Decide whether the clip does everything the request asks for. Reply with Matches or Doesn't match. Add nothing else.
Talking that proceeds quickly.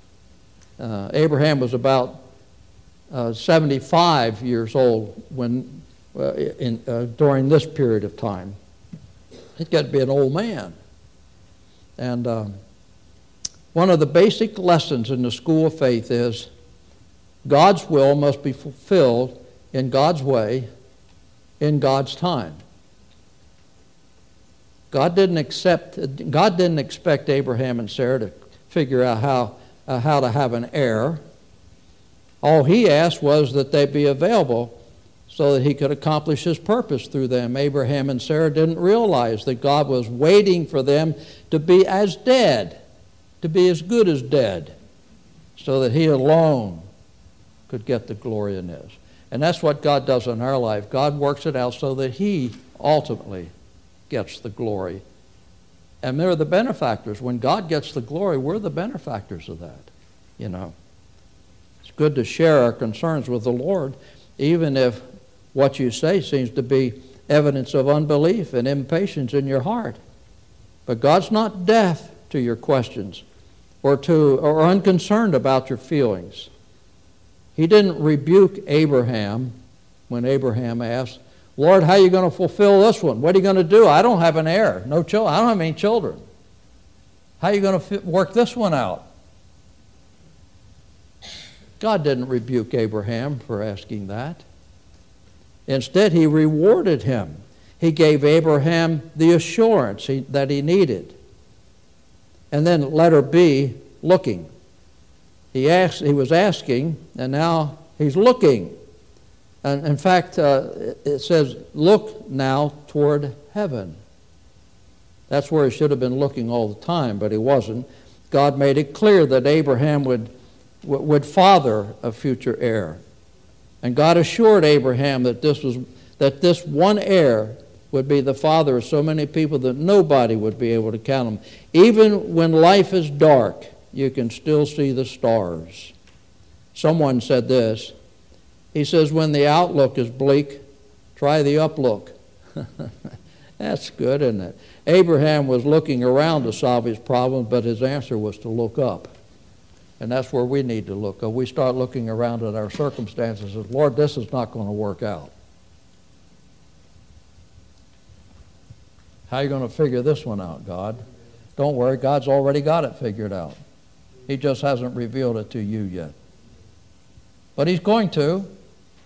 Doesn't match